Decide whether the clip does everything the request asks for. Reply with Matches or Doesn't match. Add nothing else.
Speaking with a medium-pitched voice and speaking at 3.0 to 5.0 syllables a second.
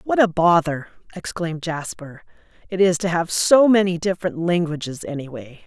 Doesn't match